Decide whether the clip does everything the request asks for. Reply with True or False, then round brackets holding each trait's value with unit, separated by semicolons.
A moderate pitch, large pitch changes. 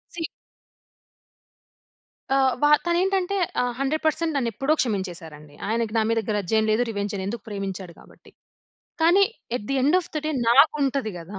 False (235 Hz; 7.2 semitones)